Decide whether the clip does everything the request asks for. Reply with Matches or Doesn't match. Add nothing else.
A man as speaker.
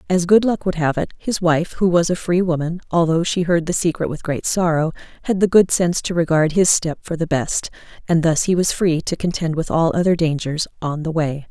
Doesn't match